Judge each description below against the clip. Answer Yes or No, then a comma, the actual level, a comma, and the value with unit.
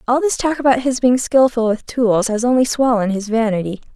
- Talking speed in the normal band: No, fast, 210 wpm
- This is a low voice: No, high, 240 Hz